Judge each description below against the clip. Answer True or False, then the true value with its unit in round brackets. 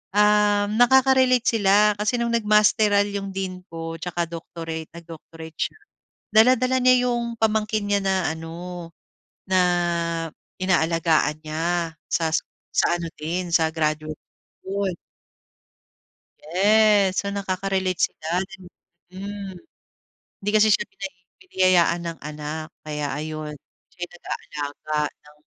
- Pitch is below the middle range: False (185 Hz)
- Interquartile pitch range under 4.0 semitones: False (4.3 semitones)